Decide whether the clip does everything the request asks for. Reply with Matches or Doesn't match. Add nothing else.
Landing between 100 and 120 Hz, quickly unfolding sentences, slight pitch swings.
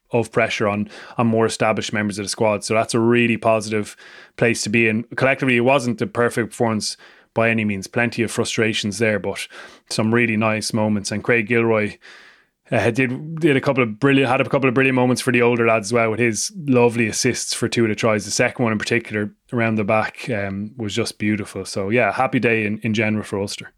Matches